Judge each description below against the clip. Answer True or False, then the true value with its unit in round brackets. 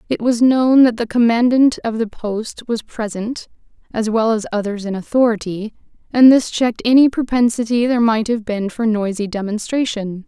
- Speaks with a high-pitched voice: True (225 Hz)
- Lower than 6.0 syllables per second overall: True (5.1 syllables/s)